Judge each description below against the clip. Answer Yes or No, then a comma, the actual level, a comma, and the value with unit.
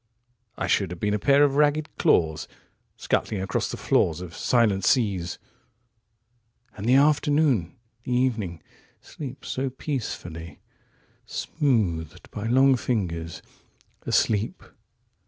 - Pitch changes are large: Yes, wide, 7.5 semitones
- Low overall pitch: Yes, low, 110 Hz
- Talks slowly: Yes, slow, 100 wpm